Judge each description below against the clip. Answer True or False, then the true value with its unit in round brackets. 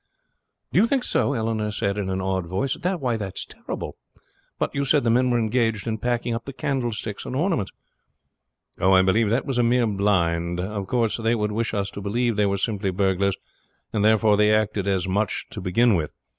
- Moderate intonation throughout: True (3.4 semitones)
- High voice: False (110 Hz)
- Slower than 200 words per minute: False (205 wpm)